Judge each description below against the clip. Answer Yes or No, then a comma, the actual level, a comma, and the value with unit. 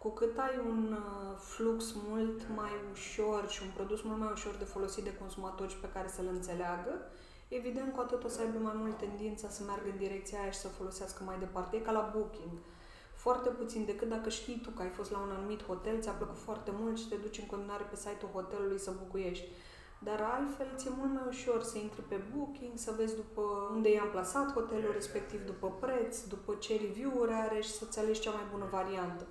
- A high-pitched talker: Yes, high, 210 Hz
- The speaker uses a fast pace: Yes, fast, 210 wpm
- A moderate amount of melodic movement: No, narrow, 2.2 semitones